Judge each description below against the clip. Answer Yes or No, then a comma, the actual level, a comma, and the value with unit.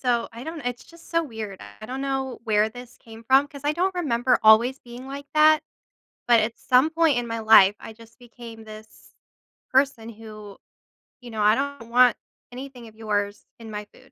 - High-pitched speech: Yes, high, 240 Hz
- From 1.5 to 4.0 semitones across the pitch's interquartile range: Yes, average, 3.5 semitones